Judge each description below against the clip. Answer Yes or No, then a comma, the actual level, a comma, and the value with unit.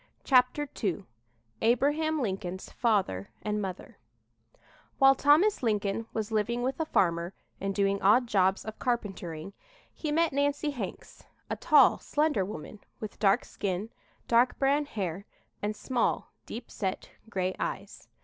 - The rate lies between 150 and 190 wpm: No, slow, 135 wpm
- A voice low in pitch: No, high, 220 Hz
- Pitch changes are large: Yes, wide, 5.7 semitones